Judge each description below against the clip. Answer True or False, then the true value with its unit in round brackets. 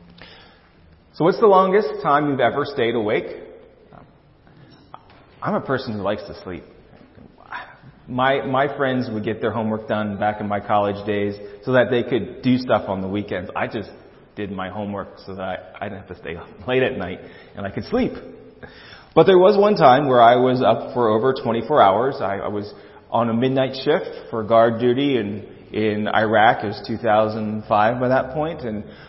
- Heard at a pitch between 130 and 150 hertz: False (115 Hz)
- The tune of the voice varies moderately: True (4.4 semitones)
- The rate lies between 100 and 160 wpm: False (190 wpm)